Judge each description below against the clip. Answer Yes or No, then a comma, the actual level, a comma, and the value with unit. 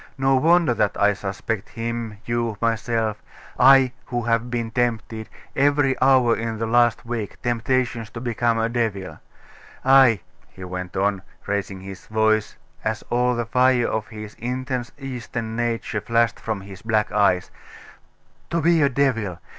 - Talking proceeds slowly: No, average, 150 wpm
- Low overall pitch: Yes, low, 115 Hz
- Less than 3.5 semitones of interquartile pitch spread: Yes, narrow, 2.6 semitones